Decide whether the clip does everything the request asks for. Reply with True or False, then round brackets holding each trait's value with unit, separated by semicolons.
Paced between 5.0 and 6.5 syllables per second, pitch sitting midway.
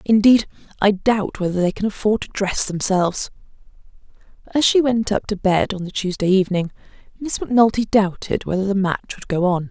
False (5.3 syllables/s; 200 Hz)